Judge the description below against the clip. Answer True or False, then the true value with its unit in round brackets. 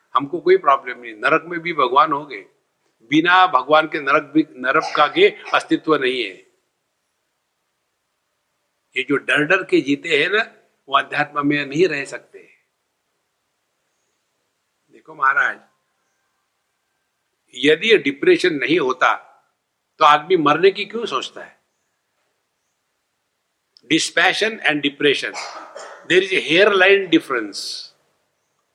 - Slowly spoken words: True (115 wpm)